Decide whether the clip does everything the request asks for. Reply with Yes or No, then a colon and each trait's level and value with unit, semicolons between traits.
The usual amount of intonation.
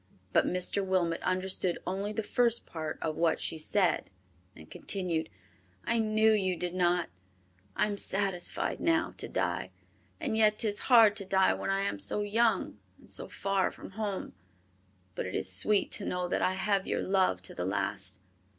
Yes: average, 3.5 semitones